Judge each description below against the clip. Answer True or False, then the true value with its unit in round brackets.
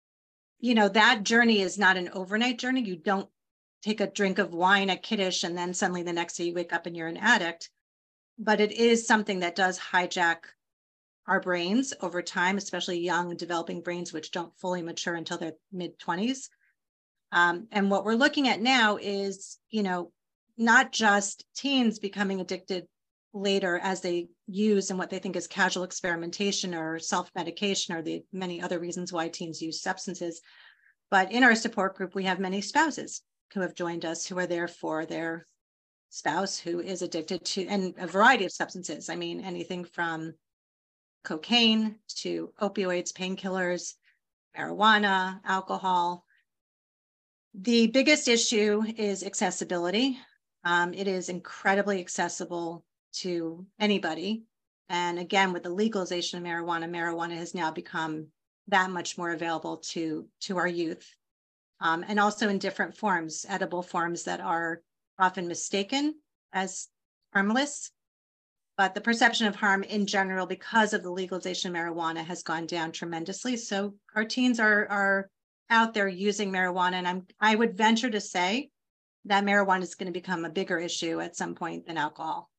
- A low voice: False (185 Hz)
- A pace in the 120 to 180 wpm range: True (160 wpm)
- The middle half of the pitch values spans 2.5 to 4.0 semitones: True (3.0 semitones)